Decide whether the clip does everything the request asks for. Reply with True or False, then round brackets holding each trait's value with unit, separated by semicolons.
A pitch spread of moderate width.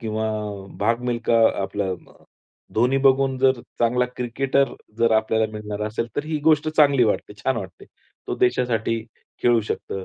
True (3.4 semitones)